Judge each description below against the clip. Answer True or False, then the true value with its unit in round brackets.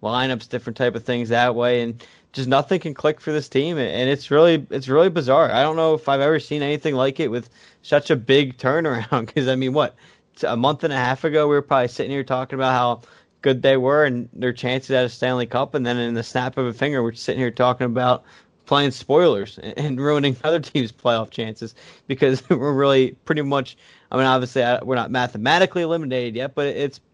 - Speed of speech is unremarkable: False (220 wpm)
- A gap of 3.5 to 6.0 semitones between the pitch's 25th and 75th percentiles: False (2.7 semitones)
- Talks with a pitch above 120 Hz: True (130 Hz)